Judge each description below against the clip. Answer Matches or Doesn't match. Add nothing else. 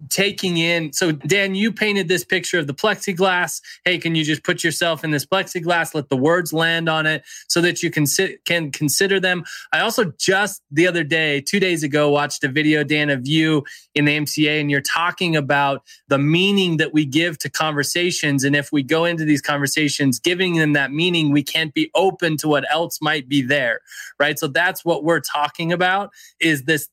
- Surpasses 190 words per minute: Matches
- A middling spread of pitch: Matches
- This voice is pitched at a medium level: Matches